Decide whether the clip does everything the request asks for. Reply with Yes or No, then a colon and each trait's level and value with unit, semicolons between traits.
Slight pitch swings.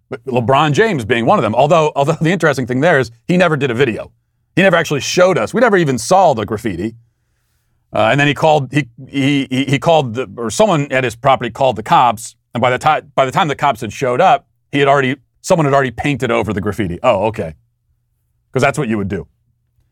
No: average, 3.7 semitones